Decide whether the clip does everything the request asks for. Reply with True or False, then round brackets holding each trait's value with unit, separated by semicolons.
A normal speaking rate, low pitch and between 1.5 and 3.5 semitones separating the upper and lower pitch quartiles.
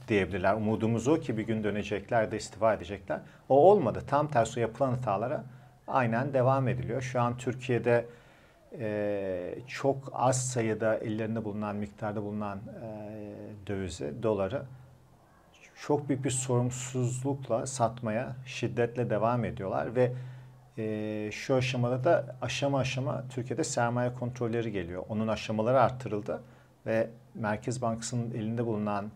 True (125 wpm; 115 Hz; 2.9 semitones)